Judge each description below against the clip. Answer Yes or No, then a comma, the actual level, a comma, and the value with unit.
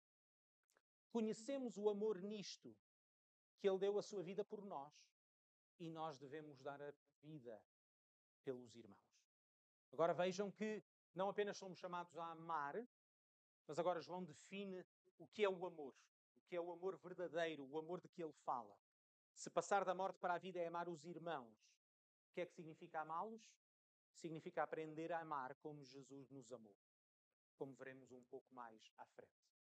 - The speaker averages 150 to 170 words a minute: Yes, average, 165 wpm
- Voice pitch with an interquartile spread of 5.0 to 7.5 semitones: Yes, wide, 5.5 semitones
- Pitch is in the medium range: Yes, medium, 165 Hz